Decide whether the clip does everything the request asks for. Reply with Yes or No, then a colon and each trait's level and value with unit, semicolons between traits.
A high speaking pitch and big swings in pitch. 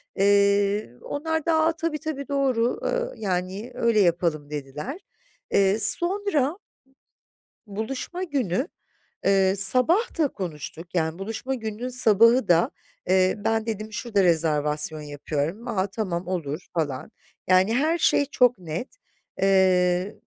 Yes: high, 205 Hz; wide, 6.5 semitones